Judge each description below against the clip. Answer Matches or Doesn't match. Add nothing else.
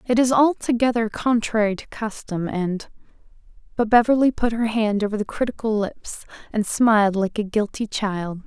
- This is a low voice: Doesn't match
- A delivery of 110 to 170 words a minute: Matches